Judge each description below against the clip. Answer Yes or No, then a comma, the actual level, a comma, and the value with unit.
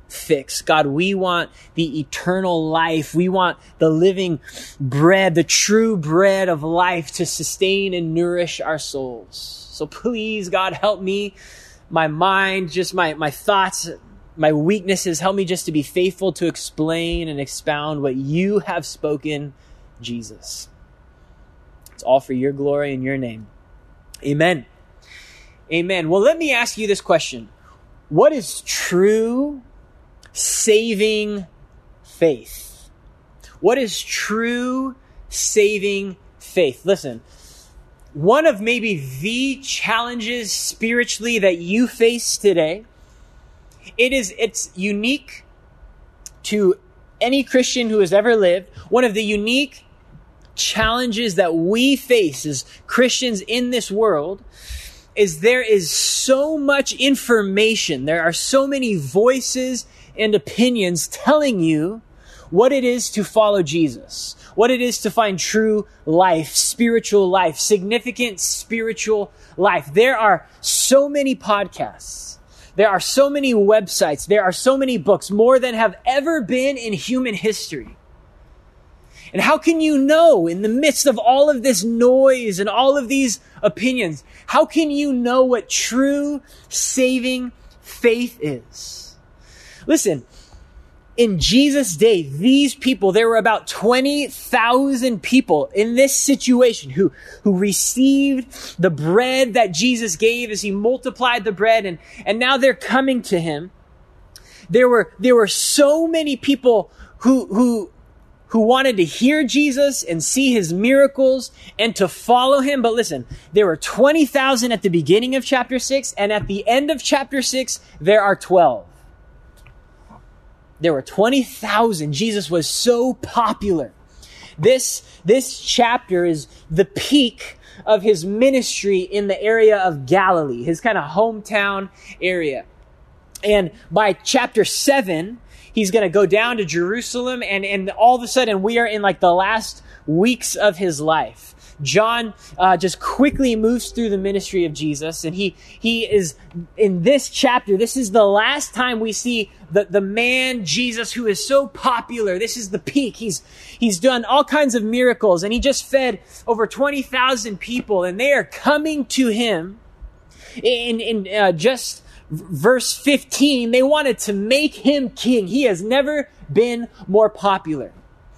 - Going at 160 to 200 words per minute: No, average, 145 wpm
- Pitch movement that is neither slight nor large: No, wide, 5.8 semitones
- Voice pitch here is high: Yes, high, 215 Hz